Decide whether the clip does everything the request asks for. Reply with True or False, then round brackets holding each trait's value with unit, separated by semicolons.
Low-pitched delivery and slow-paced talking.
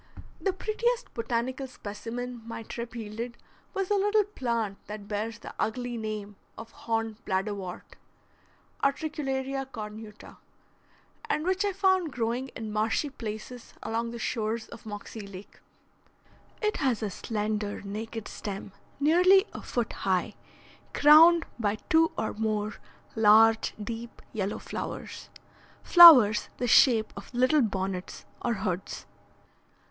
False (230 Hz; 125 wpm)